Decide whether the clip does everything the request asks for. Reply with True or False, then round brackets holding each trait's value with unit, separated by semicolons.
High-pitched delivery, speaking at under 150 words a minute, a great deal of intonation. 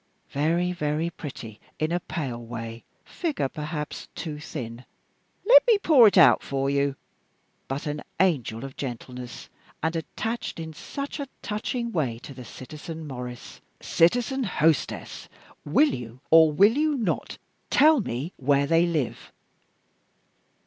False (155 Hz; 140 wpm; 5.9 semitones)